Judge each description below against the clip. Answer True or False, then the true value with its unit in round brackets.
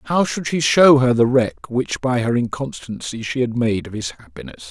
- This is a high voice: False (125 Hz)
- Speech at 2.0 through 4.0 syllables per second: False (4.7 syllables/s)